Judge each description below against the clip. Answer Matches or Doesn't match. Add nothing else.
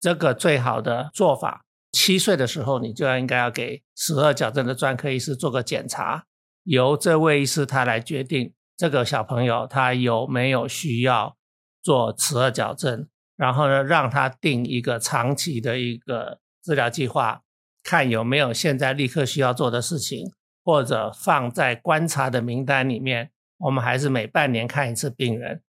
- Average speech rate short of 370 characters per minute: Matches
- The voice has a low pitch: Matches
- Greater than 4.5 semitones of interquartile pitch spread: Doesn't match